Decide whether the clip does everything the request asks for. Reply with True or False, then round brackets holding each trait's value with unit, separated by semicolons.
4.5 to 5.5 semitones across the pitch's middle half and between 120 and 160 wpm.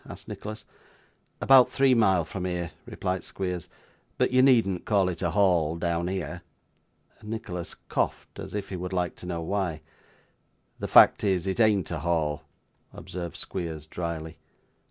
False (2.9 semitones; 155 wpm)